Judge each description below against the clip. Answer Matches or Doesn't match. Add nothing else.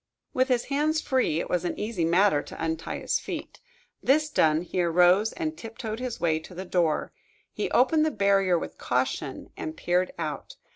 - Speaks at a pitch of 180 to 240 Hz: Matches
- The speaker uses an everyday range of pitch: Doesn't match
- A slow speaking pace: Doesn't match